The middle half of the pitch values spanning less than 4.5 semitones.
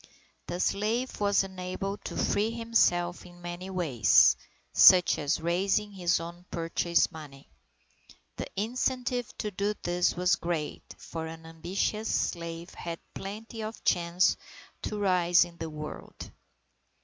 Yes: average, 3.2 semitones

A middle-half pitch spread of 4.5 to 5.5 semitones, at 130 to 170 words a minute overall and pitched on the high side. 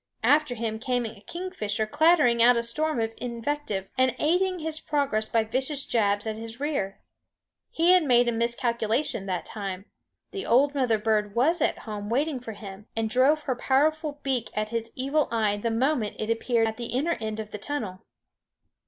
No: average, 5.0 semitones; average, 185 wpm; high, 235 Hz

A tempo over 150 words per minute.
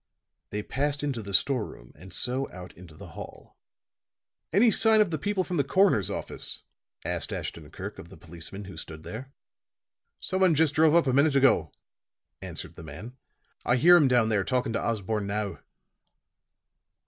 Yes: average, 170 wpm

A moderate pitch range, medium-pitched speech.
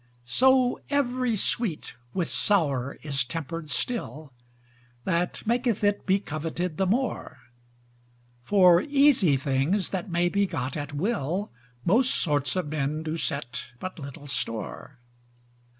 No: wide, 6.2 semitones; medium, 170 Hz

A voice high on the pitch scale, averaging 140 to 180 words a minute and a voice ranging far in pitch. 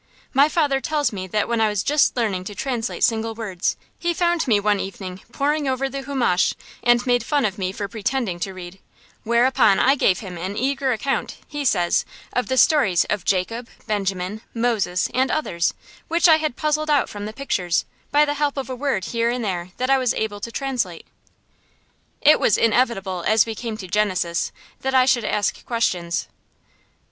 No: high, 230 Hz; average, 190 wpm; wide, 5.7 semitones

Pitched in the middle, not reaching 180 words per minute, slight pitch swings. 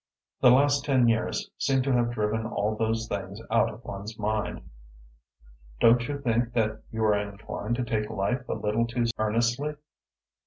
No: low, 115 Hz; average, 165 wpm; narrow, 2.3 semitones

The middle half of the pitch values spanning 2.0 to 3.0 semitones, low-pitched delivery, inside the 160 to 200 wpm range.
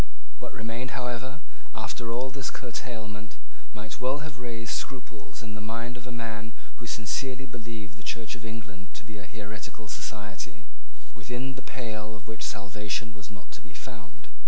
Yes: narrow, 2.5 semitones; low, 115 Hz; average, 170 wpm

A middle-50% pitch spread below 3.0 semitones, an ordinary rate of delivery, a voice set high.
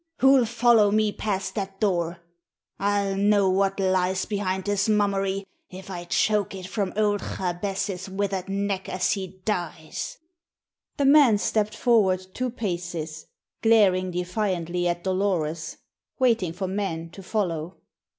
No: narrow, 2.4 semitones; slow, 130 wpm; high, 195 Hz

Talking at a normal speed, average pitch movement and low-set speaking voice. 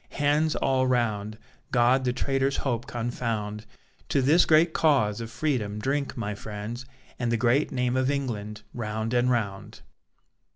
Yes: average, 150 wpm; average, 3.7 semitones; low, 120 Hz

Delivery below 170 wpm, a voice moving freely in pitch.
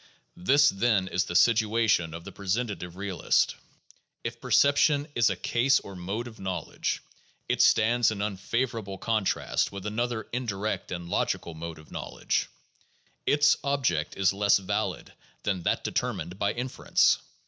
No: average, 150 wpm; average, 4.1 semitones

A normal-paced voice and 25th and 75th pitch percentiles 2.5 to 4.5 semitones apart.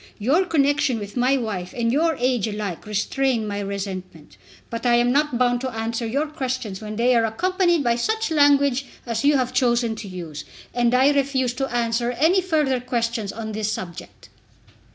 Yes: average, 180 wpm; average, 3.8 semitones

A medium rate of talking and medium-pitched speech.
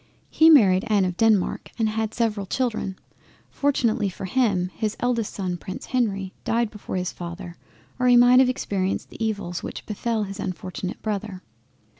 No: average, 165 wpm; high, 210 Hz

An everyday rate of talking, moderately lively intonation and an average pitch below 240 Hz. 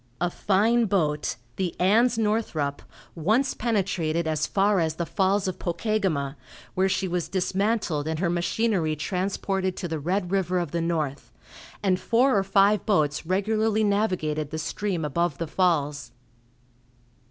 Yes: average, 145 wpm; average, 4.3 semitones; medium, 185 Hz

